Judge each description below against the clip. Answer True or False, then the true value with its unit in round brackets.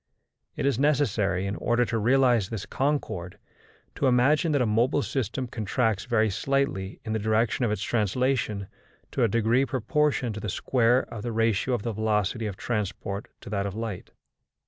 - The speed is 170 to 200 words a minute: True (175 wpm)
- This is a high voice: False (115 Hz)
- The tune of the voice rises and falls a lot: False (3.5 semitones)